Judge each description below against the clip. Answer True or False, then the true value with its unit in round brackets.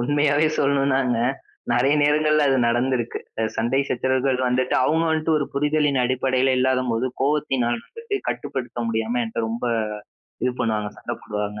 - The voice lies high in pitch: False (130 Hz)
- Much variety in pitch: False (3.3 semitones)